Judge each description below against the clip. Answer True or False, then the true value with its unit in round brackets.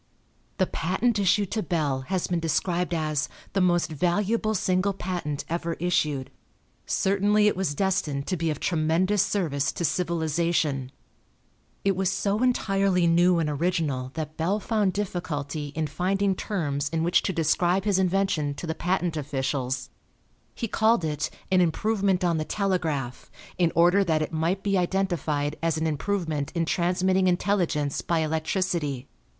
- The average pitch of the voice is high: False (175 Hz)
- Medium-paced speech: True (150 wpm)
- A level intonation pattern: False (3.7 semitones)